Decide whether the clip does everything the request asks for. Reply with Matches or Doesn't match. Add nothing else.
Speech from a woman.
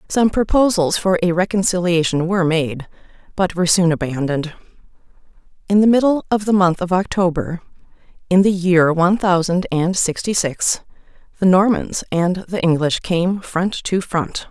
Matches